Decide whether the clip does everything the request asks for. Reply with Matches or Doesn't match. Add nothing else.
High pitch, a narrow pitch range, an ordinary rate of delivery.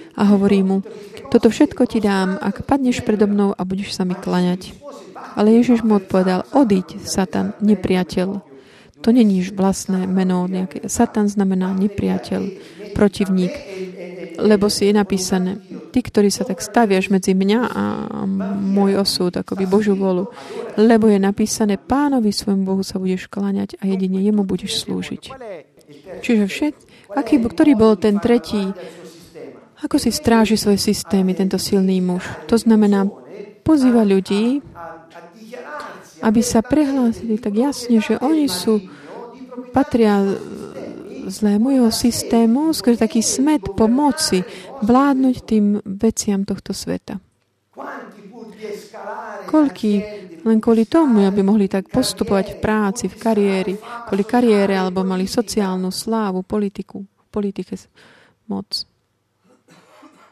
Doesn't match